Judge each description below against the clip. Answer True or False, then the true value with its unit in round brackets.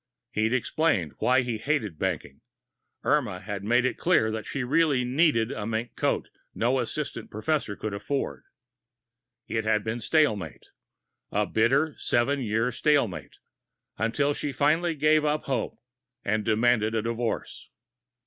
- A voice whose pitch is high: False (120 Hz)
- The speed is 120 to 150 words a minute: True (140 wpm)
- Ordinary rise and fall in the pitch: True (4.7 semitones)